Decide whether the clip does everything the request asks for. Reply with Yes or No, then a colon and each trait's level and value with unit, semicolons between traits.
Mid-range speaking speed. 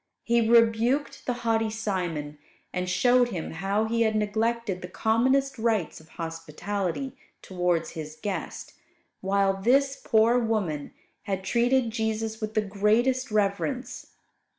No: slow, 125 wpm